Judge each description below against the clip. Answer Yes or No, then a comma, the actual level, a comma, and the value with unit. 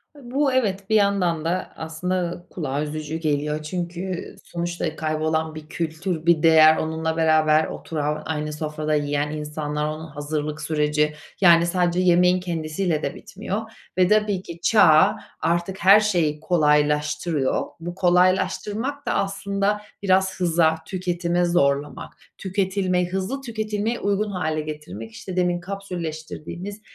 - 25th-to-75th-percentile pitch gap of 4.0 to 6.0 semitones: No, average, 3.6 semitones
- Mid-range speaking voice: Yes, medium, 170 Hz